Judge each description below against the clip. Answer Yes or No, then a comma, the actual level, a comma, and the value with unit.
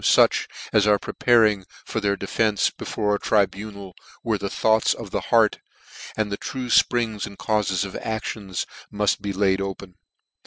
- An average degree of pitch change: No, narrow, 1.8 semitones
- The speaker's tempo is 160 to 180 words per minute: Yes, average, 170 wpm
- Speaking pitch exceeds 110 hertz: No, low, 105 Hz